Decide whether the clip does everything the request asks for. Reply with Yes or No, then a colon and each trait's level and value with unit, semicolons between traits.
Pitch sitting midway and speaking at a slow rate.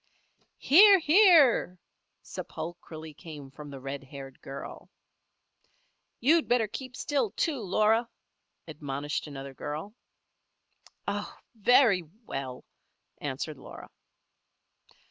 Yes: medium, 165 Hz; slow, 90 wpm